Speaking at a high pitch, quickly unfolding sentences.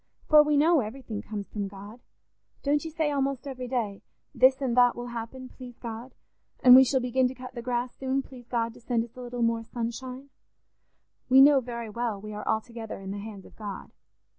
Yes: high, 245 Hz; fast, 210 wpm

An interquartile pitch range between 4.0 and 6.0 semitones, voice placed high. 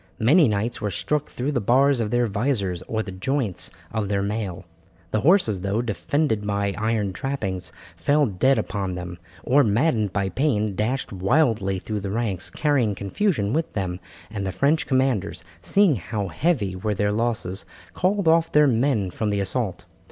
No: wide, 5.5 semitones; low, 110 Hz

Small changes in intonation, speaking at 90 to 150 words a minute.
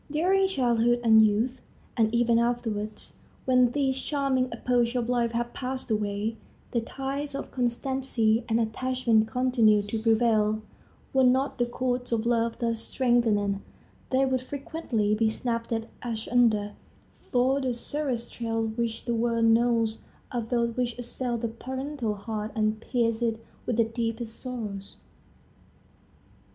Yes: narrow, 2.3 semitones; average, 140 wpm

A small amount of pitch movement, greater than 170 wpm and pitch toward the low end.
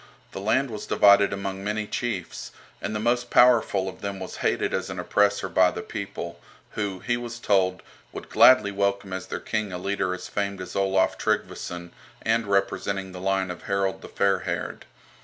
Yes: narrow, 2.0 semitones; average, 185 wpm; low, 100 Hz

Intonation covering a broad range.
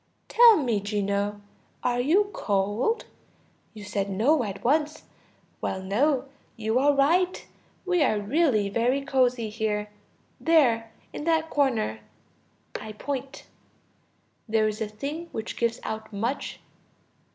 Yes: wide, 5.7 semitones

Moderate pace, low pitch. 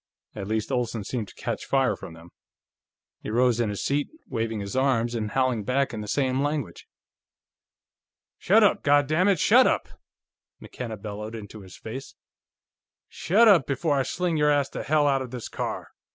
Yes: average, 175 wpm; low, 130 Hz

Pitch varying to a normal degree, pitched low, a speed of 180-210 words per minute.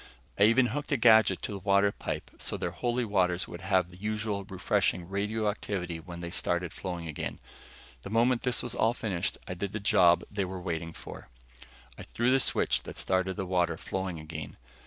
Yes: average, 3.6 semitones; very low, 95 Hz; average, 195 wpm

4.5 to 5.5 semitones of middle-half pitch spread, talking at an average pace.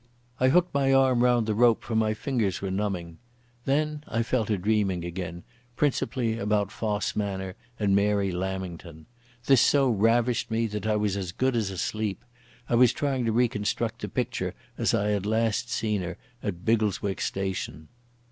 No: average, 3.7 semitones; average, 170 wpm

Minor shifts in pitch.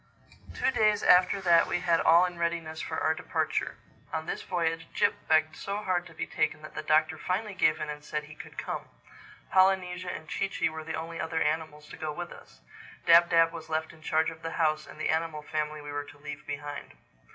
Yes: narrow, 2.1 semitones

